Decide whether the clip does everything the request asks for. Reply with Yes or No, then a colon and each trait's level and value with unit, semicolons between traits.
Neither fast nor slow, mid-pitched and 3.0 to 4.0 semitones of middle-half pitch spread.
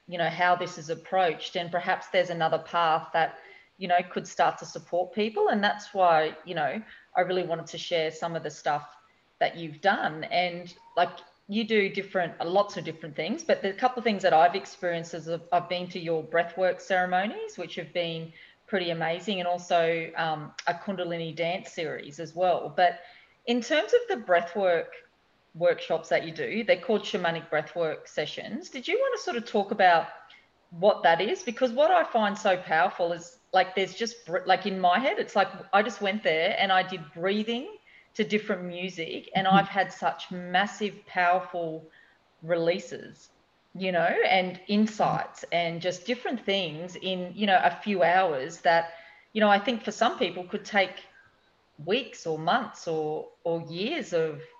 Yes: average, 185 wpm; medium, 180 Hz; average, 3.4 semitones